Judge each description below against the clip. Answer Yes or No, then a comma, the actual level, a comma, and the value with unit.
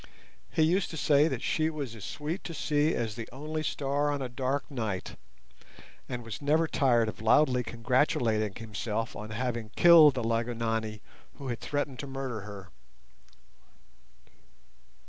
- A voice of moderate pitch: No, low, 125 Hz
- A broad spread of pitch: No, average, 4.6 semitones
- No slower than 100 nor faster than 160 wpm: Yes, average, 150 wpm